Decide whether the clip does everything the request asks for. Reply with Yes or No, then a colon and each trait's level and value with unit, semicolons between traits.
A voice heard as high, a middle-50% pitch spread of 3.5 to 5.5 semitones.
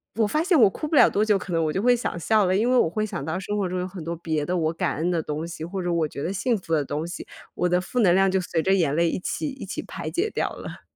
No: medium, 180 Hz; average, 4.1 semitones